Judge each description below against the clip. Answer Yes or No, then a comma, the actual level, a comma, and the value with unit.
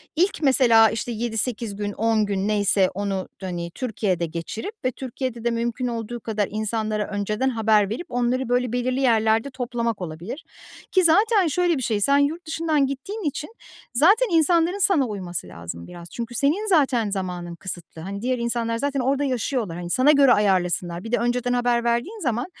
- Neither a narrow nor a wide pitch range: Yes, average, 5.0 semitones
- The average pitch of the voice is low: No, high, 235 Hz